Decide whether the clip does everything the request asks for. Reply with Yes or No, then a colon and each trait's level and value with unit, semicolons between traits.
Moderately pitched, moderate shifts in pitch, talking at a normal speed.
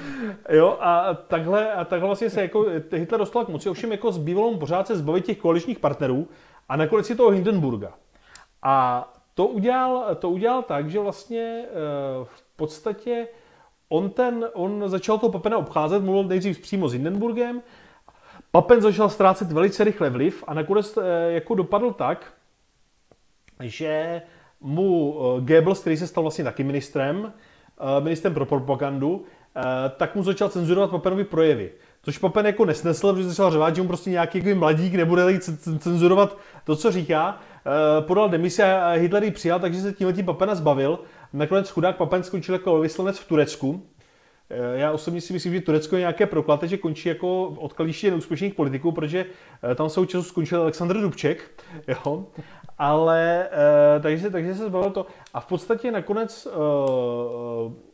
Yes: medium, 175 Hz; average, 4.4 semitones; average, 150 wpm